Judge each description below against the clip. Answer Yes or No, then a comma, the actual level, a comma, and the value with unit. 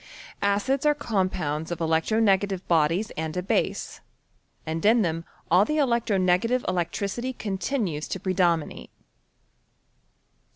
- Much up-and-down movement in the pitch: No, average, 5.0 semitones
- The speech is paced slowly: Yes, slow, 125 wpm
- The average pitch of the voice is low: No, high, 190 Hz